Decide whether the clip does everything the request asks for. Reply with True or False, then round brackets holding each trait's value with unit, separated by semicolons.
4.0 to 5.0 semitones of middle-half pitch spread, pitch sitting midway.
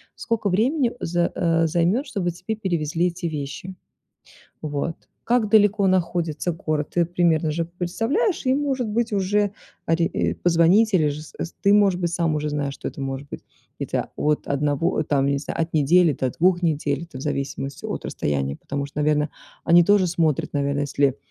True (4.3 semitones; 170 Hz)